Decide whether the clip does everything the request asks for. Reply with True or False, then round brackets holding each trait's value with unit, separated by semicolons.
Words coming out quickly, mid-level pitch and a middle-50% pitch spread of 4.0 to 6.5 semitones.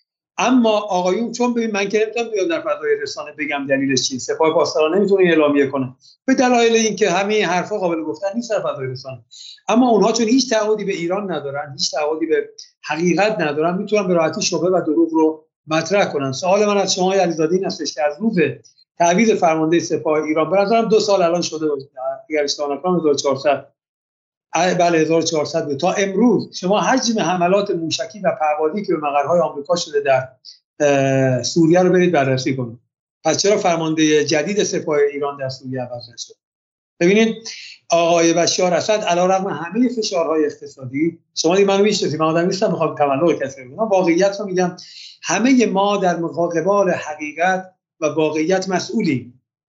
True (160 wpm; 170 Hz; 4.9 semitones)